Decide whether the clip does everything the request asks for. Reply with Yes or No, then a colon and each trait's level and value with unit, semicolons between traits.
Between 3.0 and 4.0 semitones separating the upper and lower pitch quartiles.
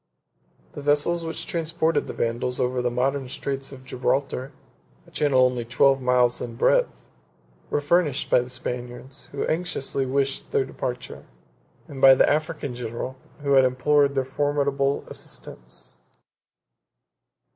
No: narrow, 2.4 semitones